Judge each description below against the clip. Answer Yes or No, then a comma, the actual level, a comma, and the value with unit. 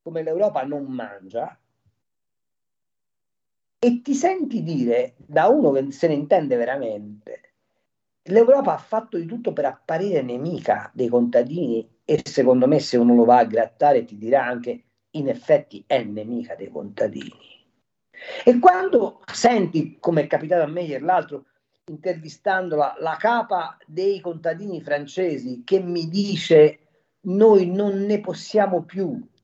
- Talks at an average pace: Yes, average, 135 wpm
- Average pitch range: No, wide, 6.7 semitones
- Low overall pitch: No, medium, 165 Hz